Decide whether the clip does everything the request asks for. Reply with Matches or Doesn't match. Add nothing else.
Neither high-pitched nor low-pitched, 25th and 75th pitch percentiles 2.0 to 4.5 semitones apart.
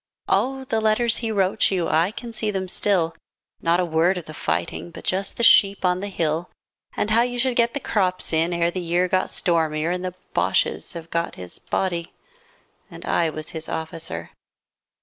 Matches